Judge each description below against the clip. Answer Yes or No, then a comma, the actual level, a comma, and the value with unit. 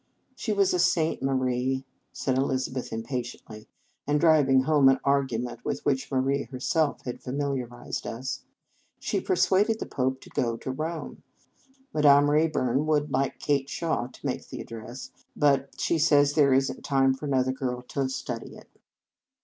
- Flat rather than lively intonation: Yes, narrow, 2.3 semitones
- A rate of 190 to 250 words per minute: No, average, 180 wpm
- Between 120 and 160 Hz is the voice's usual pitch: Yes, low, 135 Hz